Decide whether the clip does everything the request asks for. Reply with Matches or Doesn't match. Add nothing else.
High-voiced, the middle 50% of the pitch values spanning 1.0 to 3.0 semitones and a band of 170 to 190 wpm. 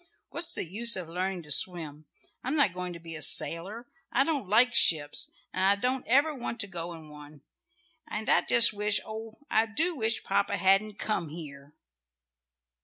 Doesn't match